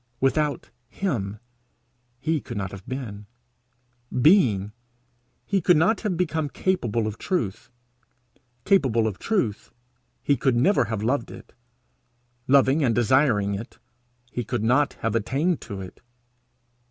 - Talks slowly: Yes, slow, 130 wpm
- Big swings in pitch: Yes, wide, 6.4 semitones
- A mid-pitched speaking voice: No, low, 130 Hz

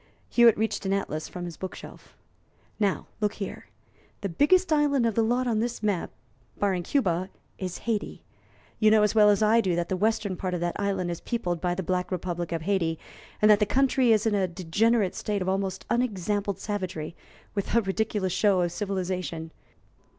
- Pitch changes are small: No, average, 3.4 semitones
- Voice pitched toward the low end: No, high, 200 Hz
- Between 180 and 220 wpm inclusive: Yes, average, 195 wpm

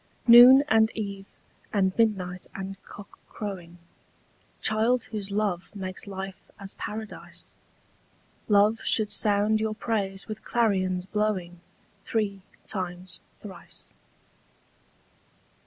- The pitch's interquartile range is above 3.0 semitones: No, narrow, 2.4 semitones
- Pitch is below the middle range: No, high, 200 Hz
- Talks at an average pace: No, slow, 100 wpm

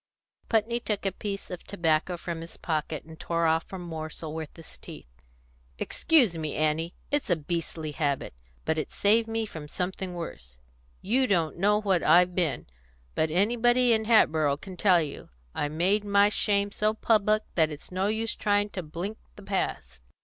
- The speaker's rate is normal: Yes, average, 175 wpm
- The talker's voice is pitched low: No, medium, 180 Hz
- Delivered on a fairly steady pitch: No, average, 4.7 semitones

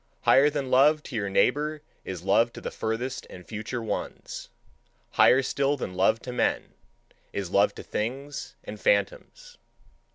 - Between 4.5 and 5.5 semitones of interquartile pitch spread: Yes, average, 5.2 semitones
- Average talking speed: Yes, average, 155 wpm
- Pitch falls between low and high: No, low, 125 Hz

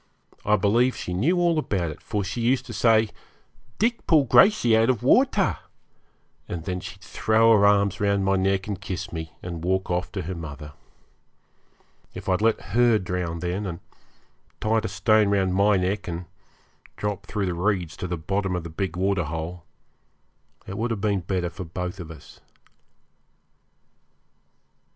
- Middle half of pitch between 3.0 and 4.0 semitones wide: Yes, average, 3.5 semitones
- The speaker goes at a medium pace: Yes, average, 170 wpm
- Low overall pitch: Yes, very low, 95 Hz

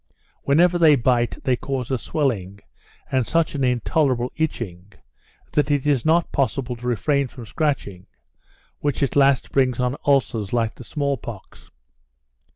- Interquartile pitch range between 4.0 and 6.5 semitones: No, average, 3.3 semitones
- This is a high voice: No, low, 130 Hz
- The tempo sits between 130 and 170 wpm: Yes, average, 150 wpm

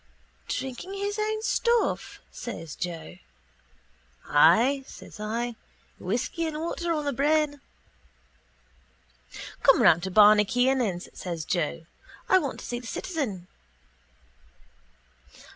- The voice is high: Yes, high, 245 Hz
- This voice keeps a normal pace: No, slow, 110 wpm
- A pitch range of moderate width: No, wide, 8.7 semitones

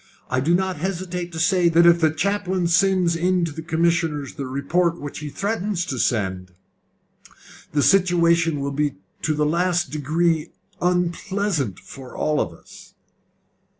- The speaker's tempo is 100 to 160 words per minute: Yes, average, 150 wpm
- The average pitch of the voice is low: No, medium, 170 Hz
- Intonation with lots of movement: No, average, 3.3 semitones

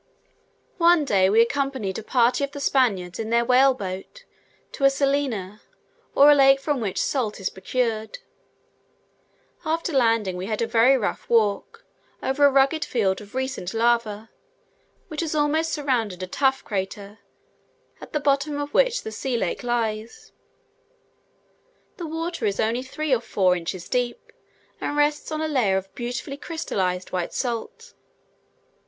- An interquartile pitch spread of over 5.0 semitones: Yes, wide, 5.4 semitones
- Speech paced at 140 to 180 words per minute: Yes, average, 150 wpm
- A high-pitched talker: Yes, high, 245 Hz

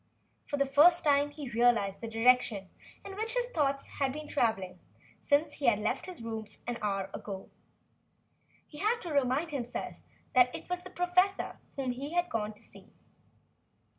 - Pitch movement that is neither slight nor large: No, wide, 5.9 semitones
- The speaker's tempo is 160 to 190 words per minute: Yes, average, 170 wpm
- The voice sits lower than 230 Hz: No, very high, 275 Hz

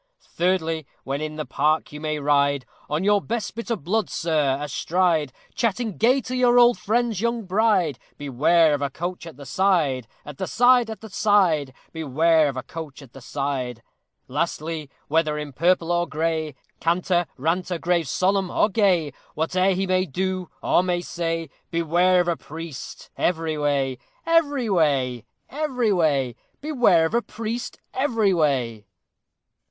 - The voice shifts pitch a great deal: No, average, 5.0 semitones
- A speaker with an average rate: Yes, average, 160 wpm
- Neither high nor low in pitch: Yes, medium, 165 Hz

